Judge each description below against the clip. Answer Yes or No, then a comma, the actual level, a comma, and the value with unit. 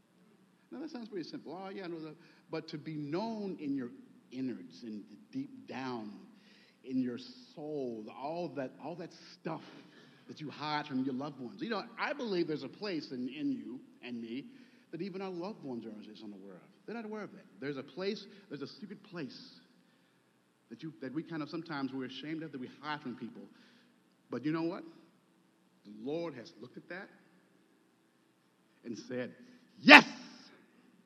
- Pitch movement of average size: No, wide, 7.8 semitones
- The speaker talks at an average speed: Yes, average, 185 wpm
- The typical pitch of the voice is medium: Yes, medium, 160 Hz